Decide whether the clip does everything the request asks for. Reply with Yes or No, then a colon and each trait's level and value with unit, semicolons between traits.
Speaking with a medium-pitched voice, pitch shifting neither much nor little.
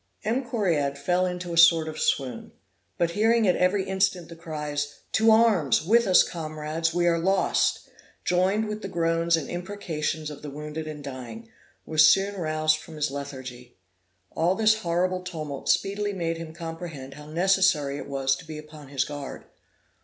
Yes: medium, 165 Hz; average, 3.8 semitones